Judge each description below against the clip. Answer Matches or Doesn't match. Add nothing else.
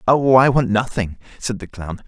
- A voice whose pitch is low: Matches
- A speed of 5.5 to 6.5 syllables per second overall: Doesn't match